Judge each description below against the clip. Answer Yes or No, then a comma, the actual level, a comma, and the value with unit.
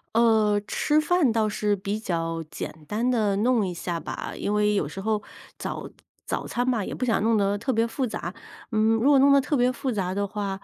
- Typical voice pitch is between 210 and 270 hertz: Yes, high, 215 Hz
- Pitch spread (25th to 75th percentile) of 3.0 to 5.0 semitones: Yes, average, 3.5 semitones